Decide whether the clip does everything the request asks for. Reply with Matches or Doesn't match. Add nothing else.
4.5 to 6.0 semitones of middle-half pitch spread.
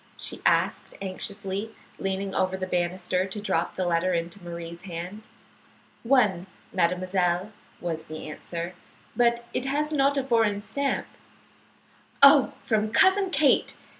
Matches